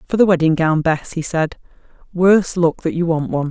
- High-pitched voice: No, medium, 165 Hz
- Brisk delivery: Yes, fast, 225 wpm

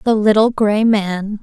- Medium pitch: No, high, 210 Hz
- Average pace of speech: Yes, average, 170 wpm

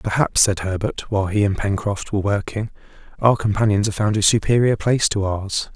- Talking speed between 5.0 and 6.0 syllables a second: Yes, 5.5 syllables/s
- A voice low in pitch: Yes, low, 105 Hz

